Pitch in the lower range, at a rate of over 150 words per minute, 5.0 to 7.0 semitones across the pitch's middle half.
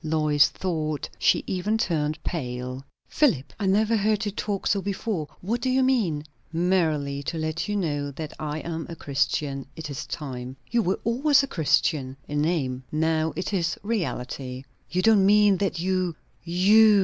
No: medium, 165 Hz; average, 170 wpm; wide, 5.5 semitones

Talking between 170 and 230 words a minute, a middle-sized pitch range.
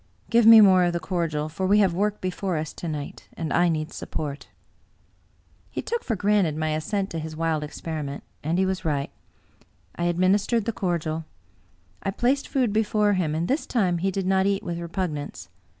Yes: average, 190 wpm; average, 4.2 semitones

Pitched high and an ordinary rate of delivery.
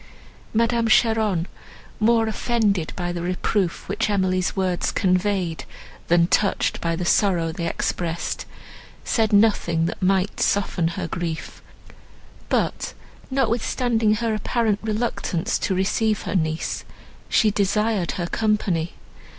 No: high, 200 Hz; slow, 120 wpm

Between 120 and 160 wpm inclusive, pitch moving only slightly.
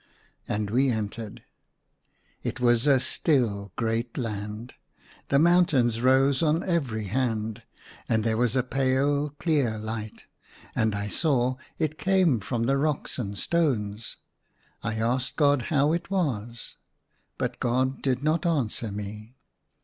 No: slow, 135 wpm; average, 4.4 semitones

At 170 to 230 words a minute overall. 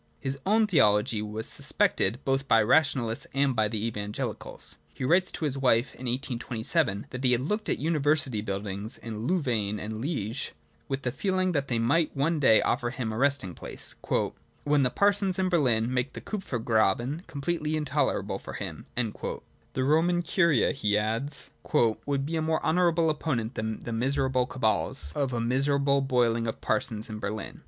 Yes: average, 180 wpm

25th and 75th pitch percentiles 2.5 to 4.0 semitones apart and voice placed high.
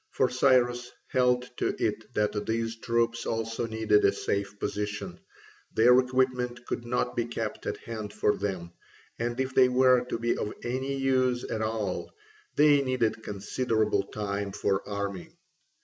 No: average, 3.0 semitones; low, 115 Hz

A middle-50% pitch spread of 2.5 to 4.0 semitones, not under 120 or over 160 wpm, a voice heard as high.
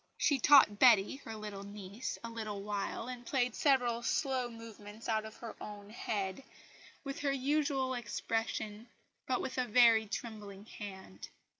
Yes: average, 3.5 semitones; average, 150 wpm; high, 225 Hz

